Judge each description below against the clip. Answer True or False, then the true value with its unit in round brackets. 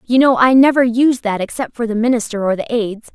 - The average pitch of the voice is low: False (235 Hz)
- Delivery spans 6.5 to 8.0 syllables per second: False (6.1 syllables/s)